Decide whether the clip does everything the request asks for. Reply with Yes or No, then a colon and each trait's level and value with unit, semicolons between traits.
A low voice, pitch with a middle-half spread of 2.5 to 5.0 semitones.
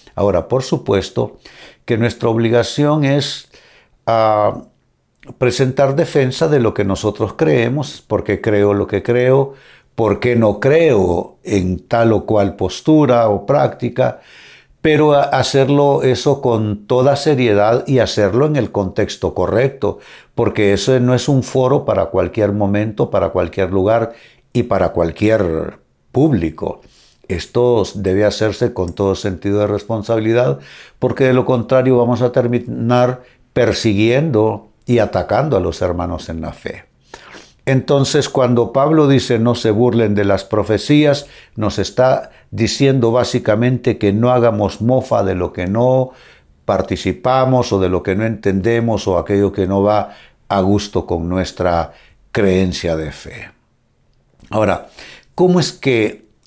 Yes: low, 115 Hz; average, 4.2 semitones